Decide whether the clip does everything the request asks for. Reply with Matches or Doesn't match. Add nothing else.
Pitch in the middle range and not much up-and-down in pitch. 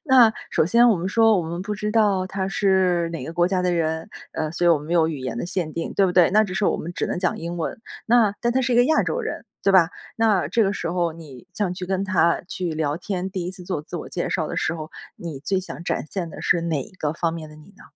Doesn't match